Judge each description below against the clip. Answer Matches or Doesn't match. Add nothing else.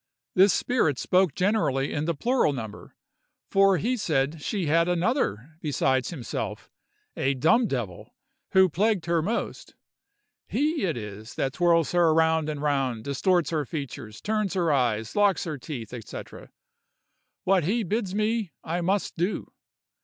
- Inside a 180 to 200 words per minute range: Doesn't match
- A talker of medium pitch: Matches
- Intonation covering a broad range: Matches